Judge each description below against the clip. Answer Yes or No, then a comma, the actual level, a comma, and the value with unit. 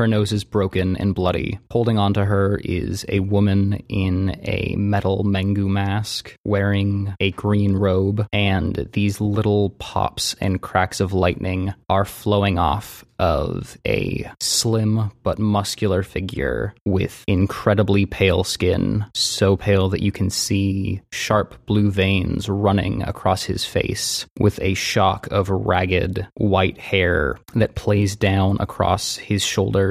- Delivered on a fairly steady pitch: Yes, narrow, 1.5 semitones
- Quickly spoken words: No, slow, 135 wpm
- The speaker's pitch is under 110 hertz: Yes, low, 100 Hz